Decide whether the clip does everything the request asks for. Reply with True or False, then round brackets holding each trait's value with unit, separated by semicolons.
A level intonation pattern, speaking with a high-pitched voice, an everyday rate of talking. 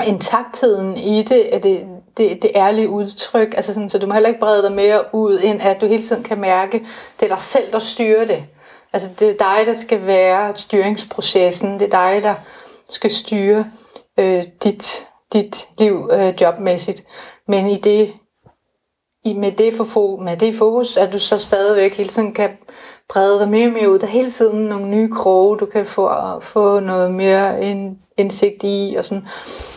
True (1.9 semitones; 205 Hz; 190 wpm)